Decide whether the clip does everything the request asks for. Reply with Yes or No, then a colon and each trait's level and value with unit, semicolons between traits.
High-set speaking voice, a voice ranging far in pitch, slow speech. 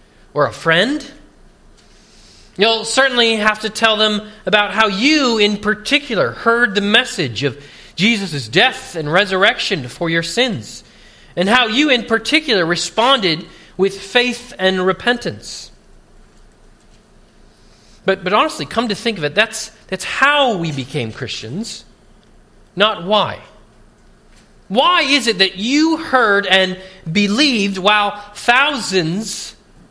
No: high, 210 Hz; average, 4.5 semitones; slow, 120 wpm